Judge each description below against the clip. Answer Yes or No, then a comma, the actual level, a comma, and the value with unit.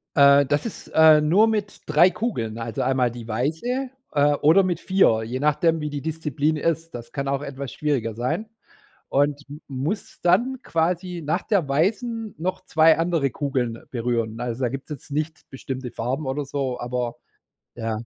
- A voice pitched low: No, medium, 145 Hz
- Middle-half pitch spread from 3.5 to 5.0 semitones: Yes, average, 4.5 semitones